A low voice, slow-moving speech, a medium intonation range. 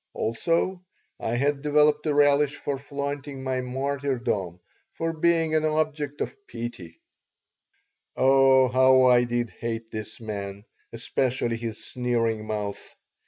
Yes: low, 130 Hz; slow, 120 wpm; average, 4.0 semitones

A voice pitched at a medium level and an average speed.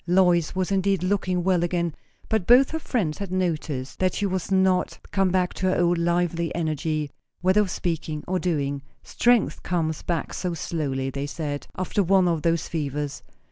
Yes: medium, 175 Hz; average, 180 wpm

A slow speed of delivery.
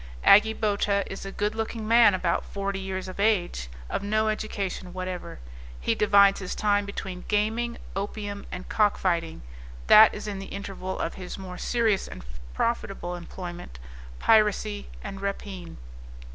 No: average, 145 wpm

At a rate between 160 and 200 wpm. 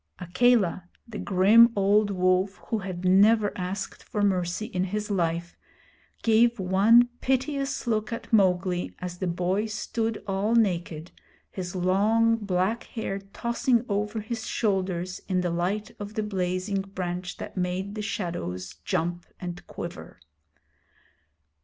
No: slow, 135 wpm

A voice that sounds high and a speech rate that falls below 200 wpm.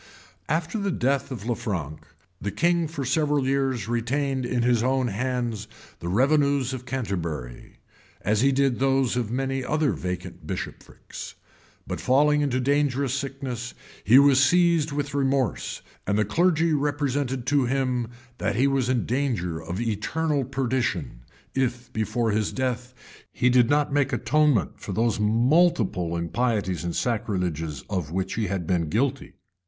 No: low, 125 Hz; average, 150 wpm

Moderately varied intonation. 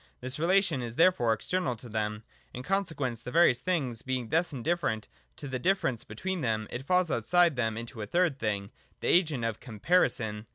No: wide, 7.4 semitones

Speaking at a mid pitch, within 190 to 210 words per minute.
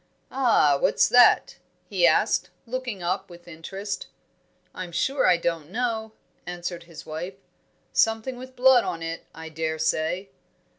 No: medium, 180 Hz; average, 140 wpm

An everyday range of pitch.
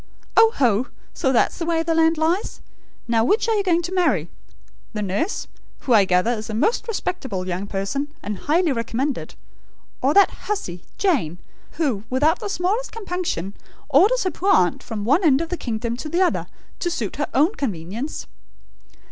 No: wide, 8.5 semitones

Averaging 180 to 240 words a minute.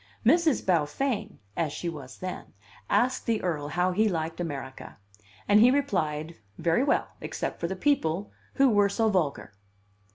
No: average, 155 wpm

